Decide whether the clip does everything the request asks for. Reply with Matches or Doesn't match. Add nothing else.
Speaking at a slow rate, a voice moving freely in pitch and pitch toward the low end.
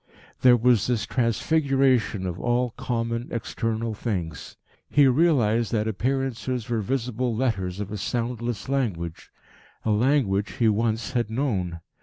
Doesn't match